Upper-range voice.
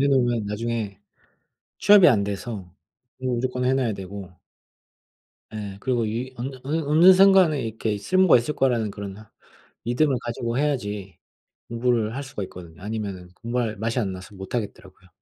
No: low, 115 Hz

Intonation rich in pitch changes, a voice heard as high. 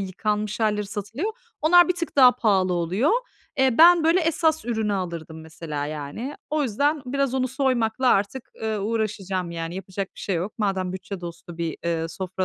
Yes: wide, 6.5 semitones; high, 210 Hz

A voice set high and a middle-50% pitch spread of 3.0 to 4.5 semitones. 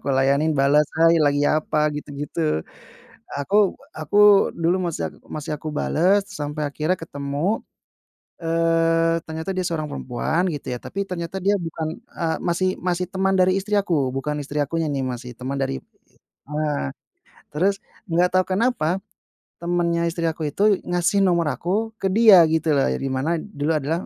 No: medium, 165 Hz; average, 3.8 semitones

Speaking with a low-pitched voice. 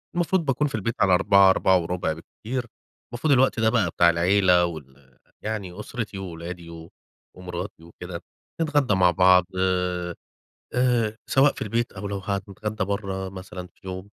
Yes: very low, 95 Hz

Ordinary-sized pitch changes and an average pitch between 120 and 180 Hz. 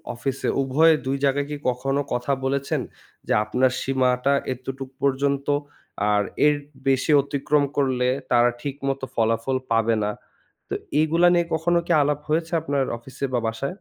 No: narrow, 2.1 semitones; low, 135 Hz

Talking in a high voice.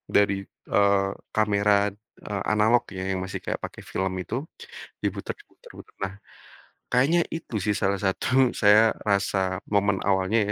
No: low, 100 Hz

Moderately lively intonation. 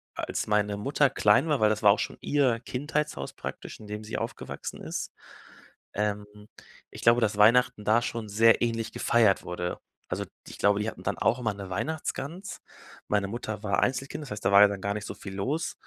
Yes: average, 3.5 semitones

